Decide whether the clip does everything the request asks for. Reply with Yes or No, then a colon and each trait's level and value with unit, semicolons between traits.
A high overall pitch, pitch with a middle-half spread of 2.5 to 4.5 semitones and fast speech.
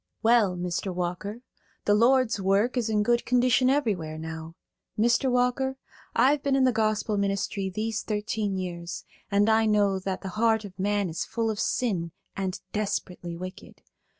No: high, 210 Hz; average, 3.9 semitones; average, 160 wpm